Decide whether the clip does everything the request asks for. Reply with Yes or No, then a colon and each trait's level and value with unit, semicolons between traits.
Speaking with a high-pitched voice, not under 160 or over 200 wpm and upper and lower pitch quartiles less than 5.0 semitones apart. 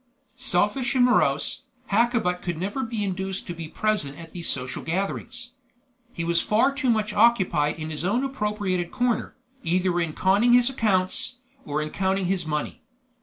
No: high, 195 Hz; average, 165 wpm; wide, 5.5 semitones